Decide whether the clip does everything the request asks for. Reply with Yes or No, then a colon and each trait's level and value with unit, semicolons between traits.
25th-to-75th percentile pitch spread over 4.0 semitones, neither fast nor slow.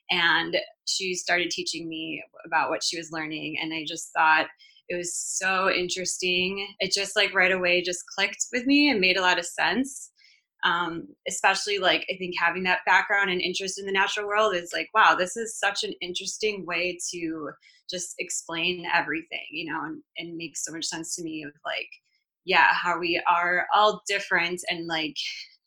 No: average, 3.5 semitones; average, 190 wpm